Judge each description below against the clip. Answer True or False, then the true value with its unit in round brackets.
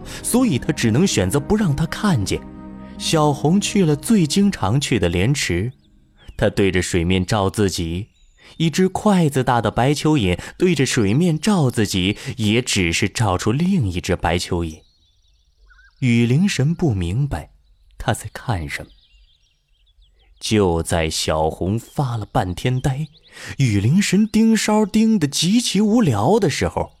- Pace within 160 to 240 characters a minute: True (205 characters per minute)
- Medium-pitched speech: False (115 Hz)